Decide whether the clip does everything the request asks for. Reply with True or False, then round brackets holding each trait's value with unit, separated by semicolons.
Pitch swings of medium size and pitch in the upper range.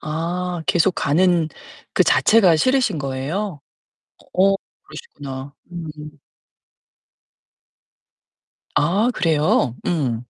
False (4.0 semitones; 165 Hz)